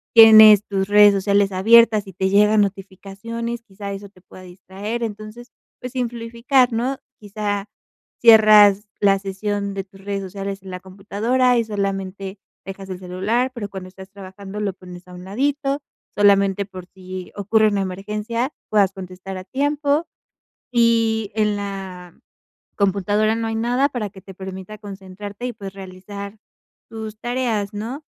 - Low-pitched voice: No, high, 205 Hz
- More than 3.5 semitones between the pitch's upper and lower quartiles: No, average, 2.7 semitones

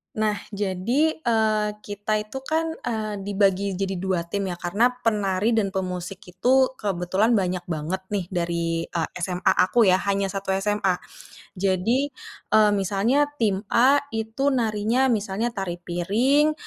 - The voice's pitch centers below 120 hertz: No, high, 205 Hz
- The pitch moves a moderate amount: Yes, average, 3.3 semitones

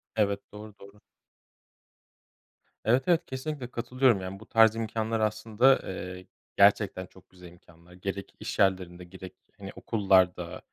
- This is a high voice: No, low, 100 Hz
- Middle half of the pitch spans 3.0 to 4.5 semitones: Yes, average, 3.5 semitones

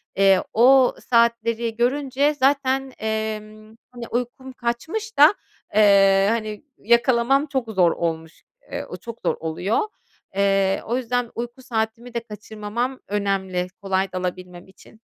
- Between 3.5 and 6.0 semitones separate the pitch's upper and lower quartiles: Yes, average, 4.0 semitones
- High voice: Yes, high, 225 Hz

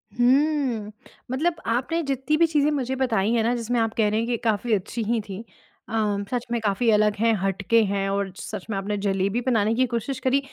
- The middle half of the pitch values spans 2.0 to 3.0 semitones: No, average, 3.7 semitones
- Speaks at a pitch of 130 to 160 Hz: No, high, 230 Hz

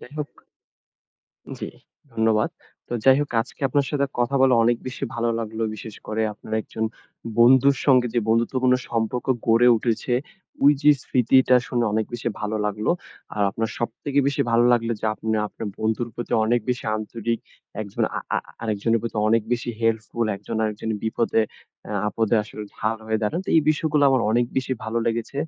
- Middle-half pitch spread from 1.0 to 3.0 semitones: Yes, narrow, 2.4 semitones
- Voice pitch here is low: Yes, low, 115 Hz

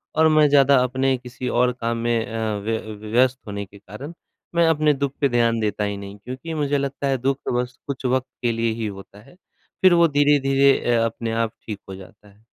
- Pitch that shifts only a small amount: No, average, 3.7 semitones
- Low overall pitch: Yes, low, 125 Hz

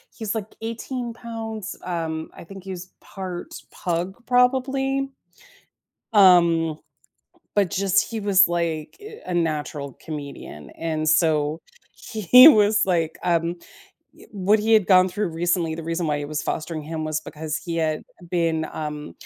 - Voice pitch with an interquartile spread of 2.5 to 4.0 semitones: No, average, 4.7 semitones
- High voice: No, medium, 175 Hz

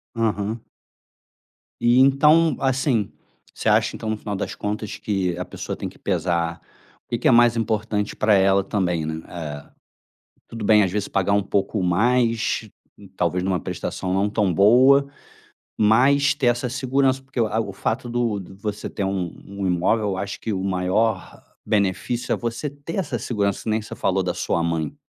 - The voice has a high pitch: No, low, 105 Hz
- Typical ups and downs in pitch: Yes, average, 3.9 semitones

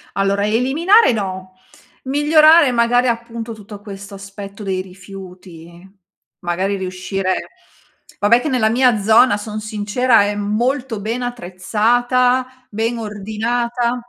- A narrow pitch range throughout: No, average, 3.7 semitones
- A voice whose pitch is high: Yes, high, 220 Hz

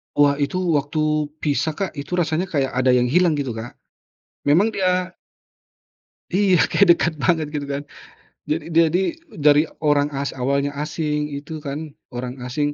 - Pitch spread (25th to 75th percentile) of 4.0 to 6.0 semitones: No, average, 3.2 semitones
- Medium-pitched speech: Yes, medium, 150 Hz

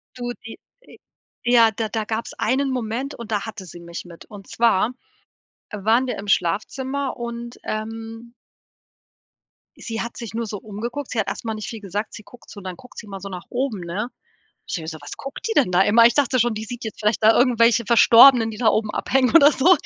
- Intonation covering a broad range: No, narrow, 2.6 semitones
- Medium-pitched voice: No, high, 225 Hz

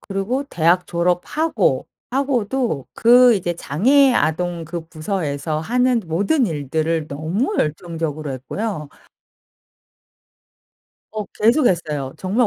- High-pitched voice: No, medium, 180 Hz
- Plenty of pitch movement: Yes, wide, 7.3 semitones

